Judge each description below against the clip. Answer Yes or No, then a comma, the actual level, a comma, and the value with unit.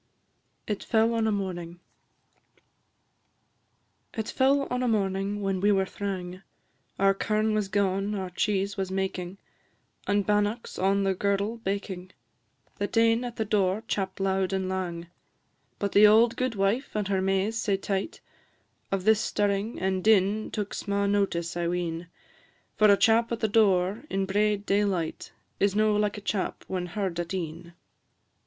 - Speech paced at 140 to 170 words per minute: Yes, average, 155 wpm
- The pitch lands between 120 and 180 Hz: No, high, 200 Hz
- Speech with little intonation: Yes, narrow, 2.0 semitones